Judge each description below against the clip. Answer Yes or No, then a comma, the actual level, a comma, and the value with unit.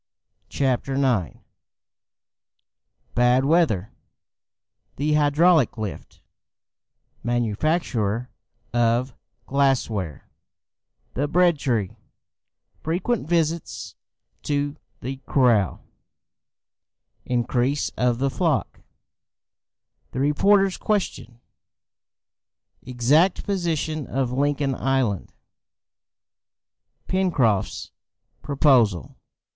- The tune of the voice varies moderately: Yes, average, 4.5 semitones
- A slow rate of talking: Yes, slow, 65 wpm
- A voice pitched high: No, low, 135 Hz